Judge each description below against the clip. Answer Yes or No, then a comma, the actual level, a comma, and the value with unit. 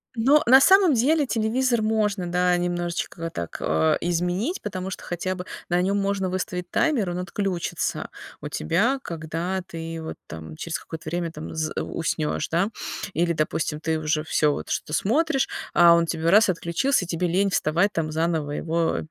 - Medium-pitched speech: Yes, medium, 175 Hz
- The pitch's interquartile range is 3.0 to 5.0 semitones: Yes, average, 3.8 semitones